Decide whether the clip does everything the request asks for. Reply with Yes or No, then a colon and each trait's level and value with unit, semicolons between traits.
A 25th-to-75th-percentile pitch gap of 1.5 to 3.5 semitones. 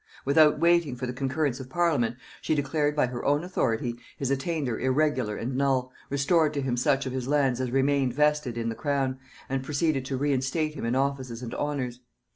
Yes: narrow, 2.6 semitones